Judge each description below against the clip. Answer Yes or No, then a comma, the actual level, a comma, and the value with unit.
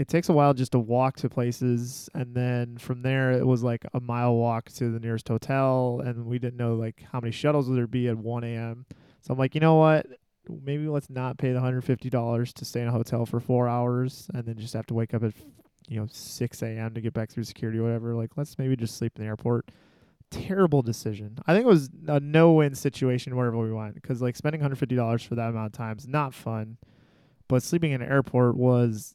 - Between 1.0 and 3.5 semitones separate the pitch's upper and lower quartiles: Yes, average, 2.8 semitones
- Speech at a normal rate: No, fast, 235 wpm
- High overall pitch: No, low, 125 Hz